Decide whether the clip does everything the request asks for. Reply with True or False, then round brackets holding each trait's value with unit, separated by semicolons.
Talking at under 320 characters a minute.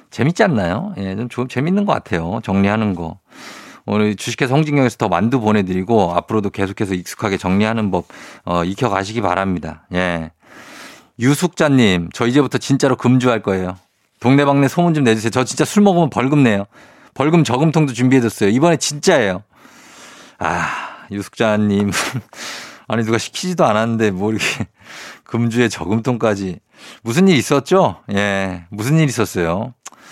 False (340 characters per minute)